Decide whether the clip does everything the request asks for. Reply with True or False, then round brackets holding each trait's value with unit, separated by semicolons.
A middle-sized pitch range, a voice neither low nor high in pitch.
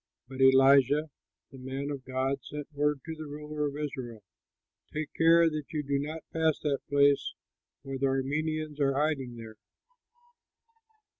False (2.2 semitones; 145 Hz)